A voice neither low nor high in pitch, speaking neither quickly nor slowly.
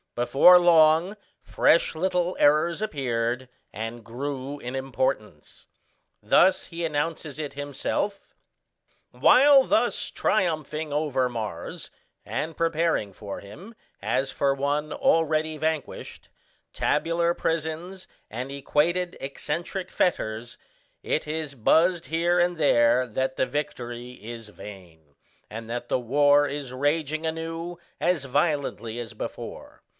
No: medium, 145 Hz; slow, 115 wpm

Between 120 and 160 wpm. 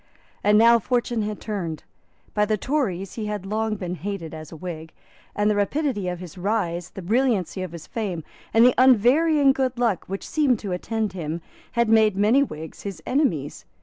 No: average, 185 wpm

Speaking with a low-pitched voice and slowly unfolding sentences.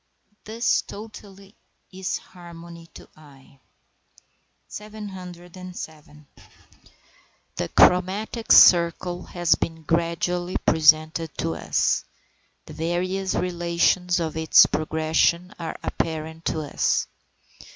No: medium, 170 Hz; slow, 90 wpm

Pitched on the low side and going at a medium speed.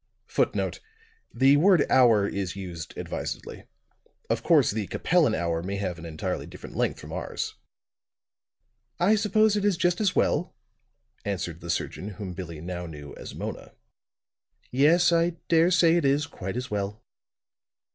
Yes: low, 115 Hz; average, 150 wpm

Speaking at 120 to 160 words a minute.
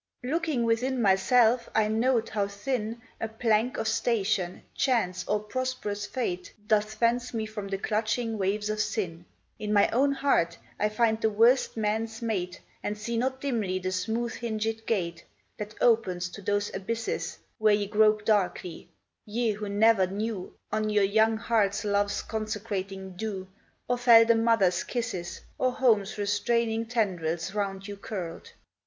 Yes: average, 155 wpm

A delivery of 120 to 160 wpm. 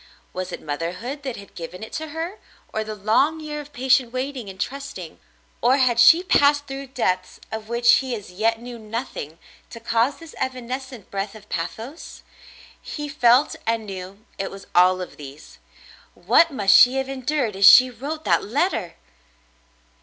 No: average, 175 wpm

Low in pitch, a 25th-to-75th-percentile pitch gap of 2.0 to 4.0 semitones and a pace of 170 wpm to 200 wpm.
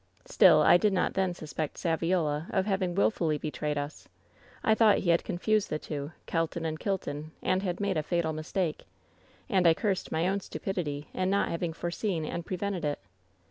No: medium, 175 Hz; average, 3.5 semitones; average, 190 wpm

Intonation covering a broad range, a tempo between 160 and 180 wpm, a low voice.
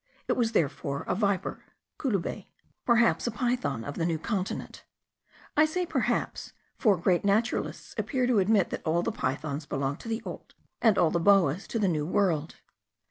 No: wide, 6.3 semitones; average, 175 wpm; high, 195 Hz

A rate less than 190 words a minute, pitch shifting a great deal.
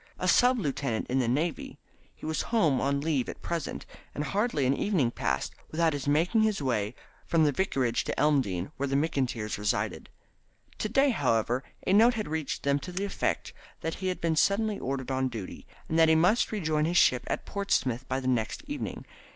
No: average, 200 wpm; wide, 6.1 semitones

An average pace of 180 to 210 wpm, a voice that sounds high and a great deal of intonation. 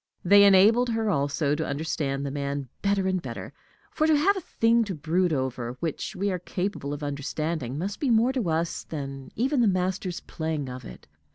No: average, 195 wpm; medium, 170 Hz; wide, 6.2 semitones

